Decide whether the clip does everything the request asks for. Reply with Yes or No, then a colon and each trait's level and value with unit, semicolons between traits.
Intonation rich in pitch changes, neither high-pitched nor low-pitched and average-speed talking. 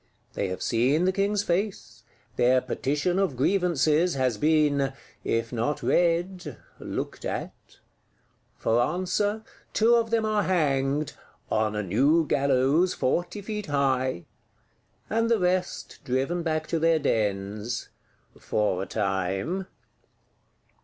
No: wide, 6.6 semitones; medium, 150 Hz; slow, 120 wpm